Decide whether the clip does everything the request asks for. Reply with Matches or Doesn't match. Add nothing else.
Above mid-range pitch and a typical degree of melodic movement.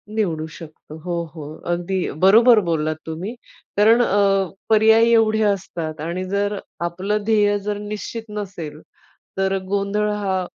Matches